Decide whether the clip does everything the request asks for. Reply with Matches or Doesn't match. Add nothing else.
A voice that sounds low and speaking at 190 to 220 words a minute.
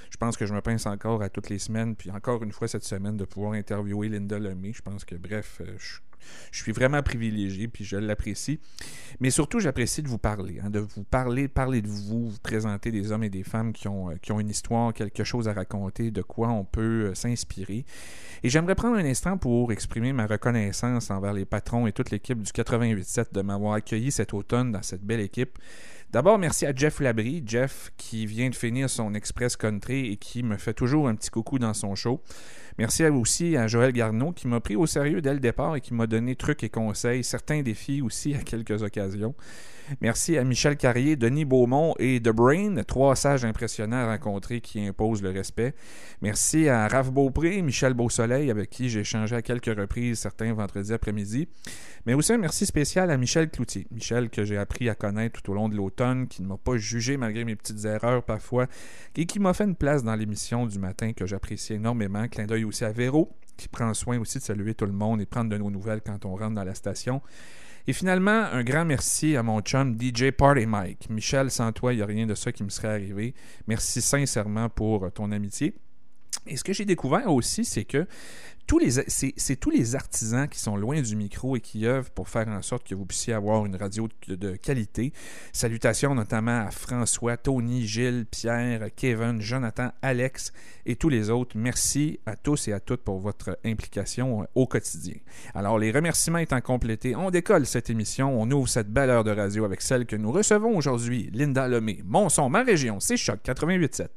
Matches